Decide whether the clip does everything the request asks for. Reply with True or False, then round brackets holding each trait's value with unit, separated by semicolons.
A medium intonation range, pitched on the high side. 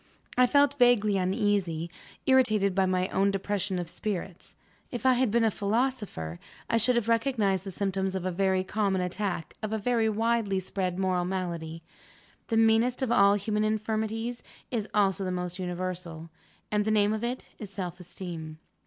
True (3.4 semitones; 200 Hz)